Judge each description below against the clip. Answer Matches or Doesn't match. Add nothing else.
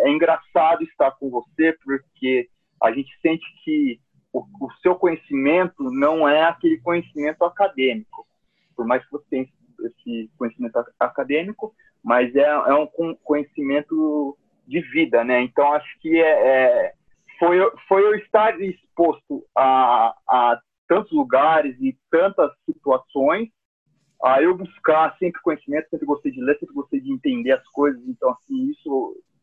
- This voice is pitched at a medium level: Matches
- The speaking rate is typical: Matches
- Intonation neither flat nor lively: Doesn't match